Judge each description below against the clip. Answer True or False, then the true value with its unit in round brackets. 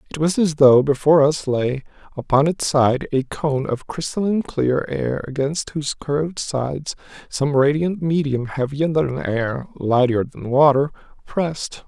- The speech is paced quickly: False (150 wpm)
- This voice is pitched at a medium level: True (145 Hz)